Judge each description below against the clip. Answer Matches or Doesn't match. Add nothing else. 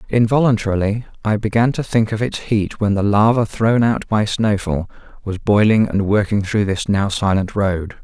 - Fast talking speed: Doesn't match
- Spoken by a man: Matches